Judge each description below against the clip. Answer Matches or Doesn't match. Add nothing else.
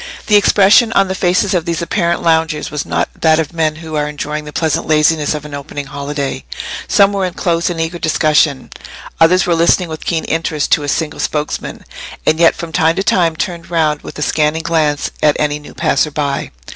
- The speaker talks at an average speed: Doesn't match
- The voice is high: Doesn't match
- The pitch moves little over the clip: Matches